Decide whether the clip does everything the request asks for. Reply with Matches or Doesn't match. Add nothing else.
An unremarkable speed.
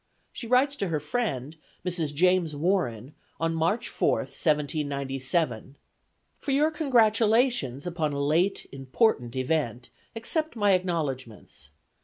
Doesn't match